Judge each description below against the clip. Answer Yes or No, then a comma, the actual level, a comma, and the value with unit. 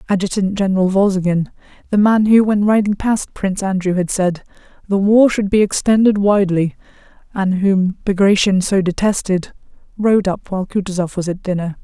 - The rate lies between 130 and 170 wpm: Yes, average, 155 wpm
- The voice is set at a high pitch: Yes, high, 195 Hz